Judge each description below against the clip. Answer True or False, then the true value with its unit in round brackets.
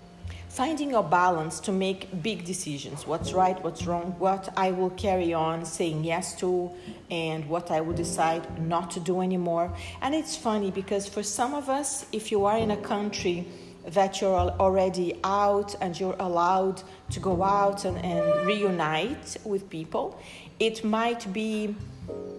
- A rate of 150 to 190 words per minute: True (160 wpm)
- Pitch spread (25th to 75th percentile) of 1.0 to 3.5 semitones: True (3.0 semitones)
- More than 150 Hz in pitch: True (190 Hz)